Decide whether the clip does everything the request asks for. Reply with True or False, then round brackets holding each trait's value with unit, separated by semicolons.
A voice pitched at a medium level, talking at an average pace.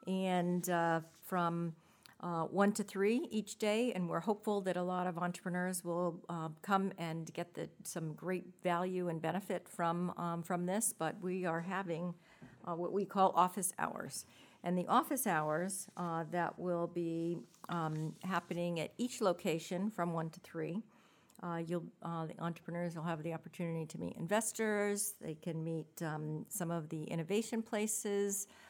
True (175 Hz; 165 wpm)